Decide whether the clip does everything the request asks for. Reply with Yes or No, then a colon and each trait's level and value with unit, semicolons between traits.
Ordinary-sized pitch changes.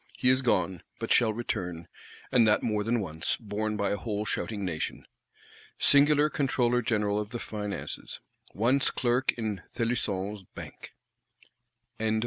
Yes: average, 3.0 semitones